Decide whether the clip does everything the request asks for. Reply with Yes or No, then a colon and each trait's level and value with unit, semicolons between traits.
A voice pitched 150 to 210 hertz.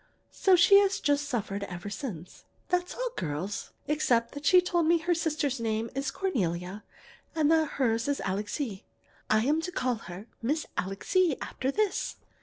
No: very high, 275 Hz